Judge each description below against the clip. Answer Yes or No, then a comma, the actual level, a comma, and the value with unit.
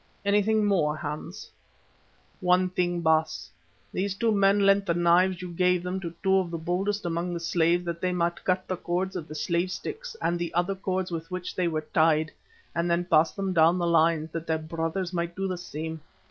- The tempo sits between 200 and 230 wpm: Yes, fast, 205 wpm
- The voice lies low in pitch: No, medium, 175 Hz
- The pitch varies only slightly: Yes, narrow, 2.1 semitones